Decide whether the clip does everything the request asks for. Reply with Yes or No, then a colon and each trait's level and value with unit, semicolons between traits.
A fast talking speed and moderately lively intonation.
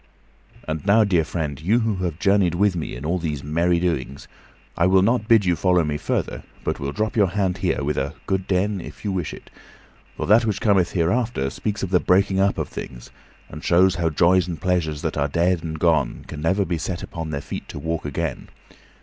Yes: fast, 220 wpm; average, 3.8 semitones